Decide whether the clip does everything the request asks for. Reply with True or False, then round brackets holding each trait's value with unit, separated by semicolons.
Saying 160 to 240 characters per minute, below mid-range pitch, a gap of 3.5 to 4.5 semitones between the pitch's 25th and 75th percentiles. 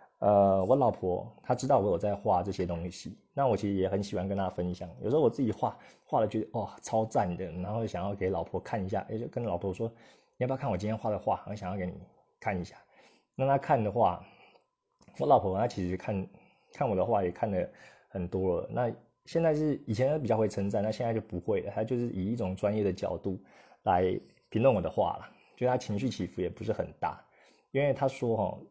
False (320 characters per minute; 105 Hz; 4.0 semitones)